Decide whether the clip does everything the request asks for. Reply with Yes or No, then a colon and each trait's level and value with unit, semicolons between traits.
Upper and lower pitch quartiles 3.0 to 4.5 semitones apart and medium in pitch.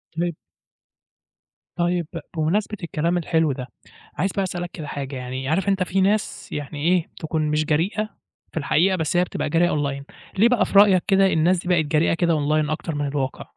Yes: average, 3.4 semitones; medium, 165 Hz